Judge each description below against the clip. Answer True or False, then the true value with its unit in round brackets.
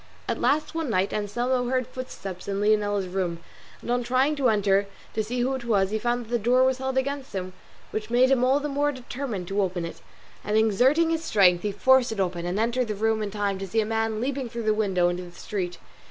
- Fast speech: True (240 wpm)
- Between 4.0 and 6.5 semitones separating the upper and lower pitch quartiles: True (4.4 semitones)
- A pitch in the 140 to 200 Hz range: False (220 Hz)